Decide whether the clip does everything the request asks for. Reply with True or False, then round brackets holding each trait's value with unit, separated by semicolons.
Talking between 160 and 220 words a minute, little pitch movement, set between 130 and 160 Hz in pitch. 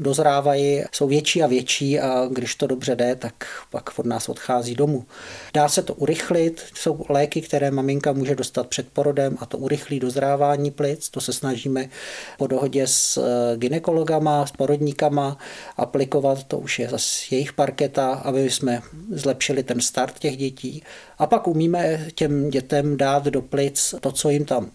True (165 wpm; 1.9 semitones; 140 Hz)